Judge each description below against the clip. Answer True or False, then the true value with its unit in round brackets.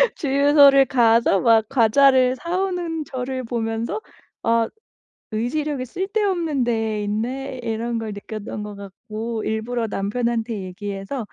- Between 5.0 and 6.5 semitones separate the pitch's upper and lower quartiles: False (3.8 semitones)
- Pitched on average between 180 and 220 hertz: False (235 Hz)